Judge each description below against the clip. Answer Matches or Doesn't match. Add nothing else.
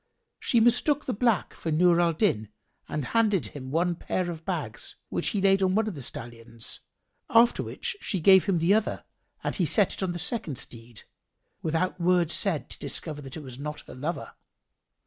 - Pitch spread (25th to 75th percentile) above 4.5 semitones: Matches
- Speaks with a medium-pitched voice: Matches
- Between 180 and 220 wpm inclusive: Matches